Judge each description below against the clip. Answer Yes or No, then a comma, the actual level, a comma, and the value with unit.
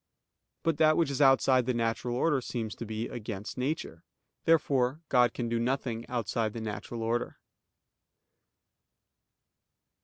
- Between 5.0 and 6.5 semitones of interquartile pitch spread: No, average, 2.9 semitones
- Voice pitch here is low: Yes, low, 120 Hz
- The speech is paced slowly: Yes, slow, 130 wpm